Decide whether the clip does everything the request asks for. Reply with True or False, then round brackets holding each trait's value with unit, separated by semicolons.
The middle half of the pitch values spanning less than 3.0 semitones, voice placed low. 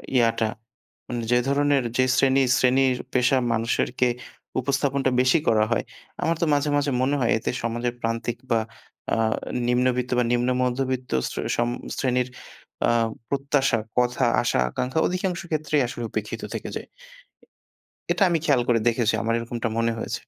True (2.6 semitones; 125 Hz)